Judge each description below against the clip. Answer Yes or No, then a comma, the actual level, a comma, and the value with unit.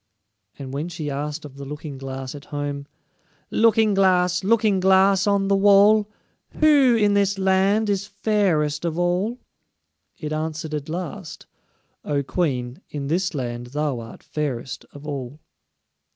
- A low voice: No, medium, 170 Hz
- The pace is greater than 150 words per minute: No, average, 145 wpm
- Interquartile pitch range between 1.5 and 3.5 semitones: No, wide, 5.6 semitones